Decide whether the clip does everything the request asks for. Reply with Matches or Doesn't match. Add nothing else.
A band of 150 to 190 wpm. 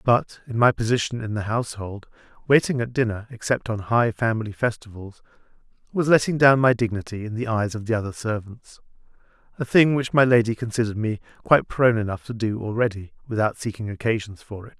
Matches